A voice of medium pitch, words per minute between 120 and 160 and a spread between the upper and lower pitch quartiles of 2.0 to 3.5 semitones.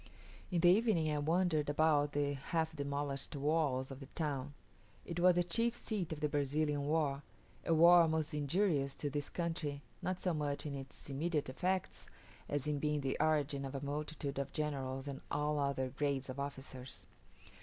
No: medium, 145 Hz; average, 175 wpm; narrow, 2.5 semitones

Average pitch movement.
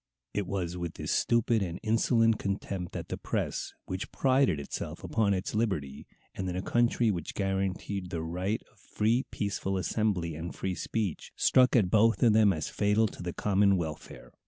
Yes: average, 3.6 semitones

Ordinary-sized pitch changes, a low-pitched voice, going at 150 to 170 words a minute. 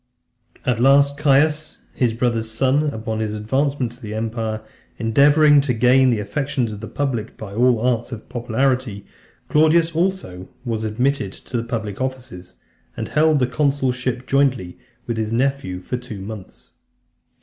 Yes: average, 3.9 semitones; low, 125 Hz; average, 155 wpm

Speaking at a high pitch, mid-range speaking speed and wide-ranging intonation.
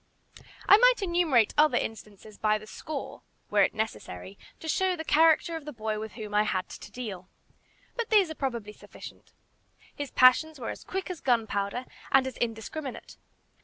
Yes: very high, 250 Hz; average, 170 wpm; wide, 6.9 semitones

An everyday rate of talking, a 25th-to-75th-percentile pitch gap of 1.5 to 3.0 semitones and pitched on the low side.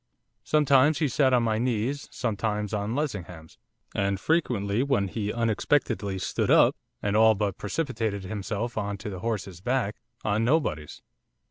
No: average, 145 wpm; average, 4.2 semitones; low, 110 Hz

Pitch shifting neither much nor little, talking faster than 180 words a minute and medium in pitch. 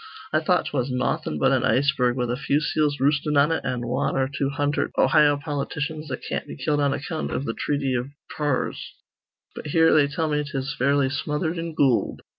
No: narrow, 2.3 semitones; fast, 205 wpm; medium, 145 Hz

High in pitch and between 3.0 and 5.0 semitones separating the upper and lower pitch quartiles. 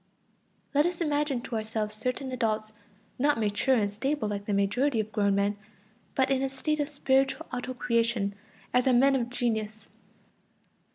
Yes: high, 245 Hz; average, 4.0 semitones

